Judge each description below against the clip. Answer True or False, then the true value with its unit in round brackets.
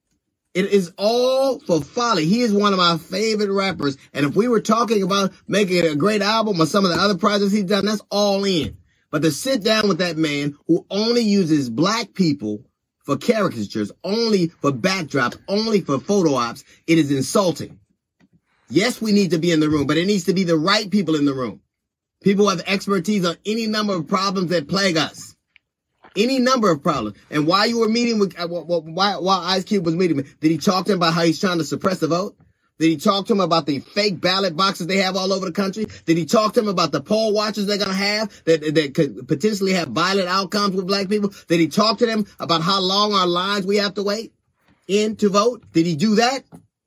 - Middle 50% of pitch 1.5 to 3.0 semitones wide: False (4.0 semitones)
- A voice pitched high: True (195 Hz)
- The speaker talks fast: True (225 wpm)